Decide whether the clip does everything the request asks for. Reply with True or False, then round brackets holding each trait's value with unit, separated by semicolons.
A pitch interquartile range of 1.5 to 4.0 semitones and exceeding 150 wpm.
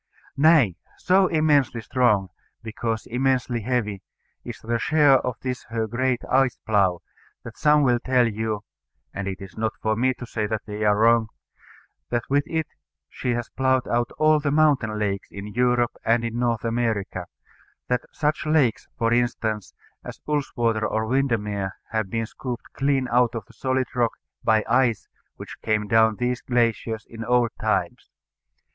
True (3.0 semitones; 165 wpm)